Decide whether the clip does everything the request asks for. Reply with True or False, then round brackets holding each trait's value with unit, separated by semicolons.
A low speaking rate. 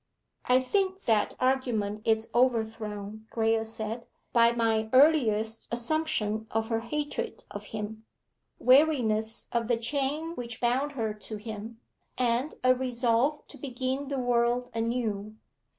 True (130 wpm)